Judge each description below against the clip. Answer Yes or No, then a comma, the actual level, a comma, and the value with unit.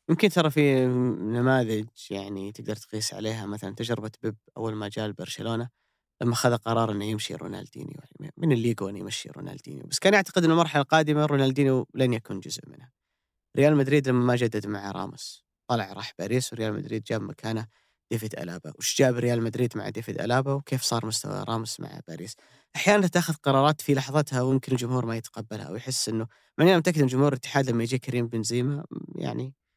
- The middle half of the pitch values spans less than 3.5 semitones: No, average, 4.6 semitones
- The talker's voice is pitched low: Yes, low, 125 Hz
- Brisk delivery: Yes, fast, 175 wpm